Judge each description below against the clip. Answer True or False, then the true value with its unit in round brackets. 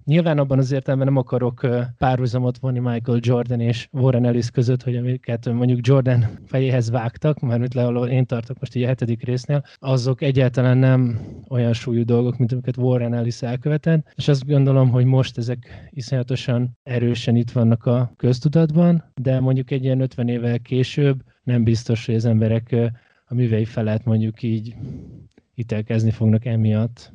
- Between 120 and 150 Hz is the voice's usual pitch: True (125 Hz)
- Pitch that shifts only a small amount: True (1.7 semitones)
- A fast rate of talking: True (160 wpm)